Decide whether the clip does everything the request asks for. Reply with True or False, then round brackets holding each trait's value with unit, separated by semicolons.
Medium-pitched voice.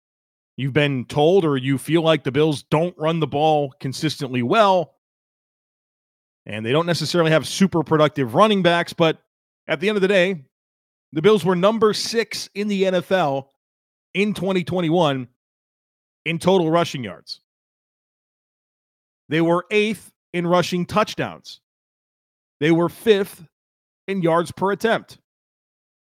True (165 Hz)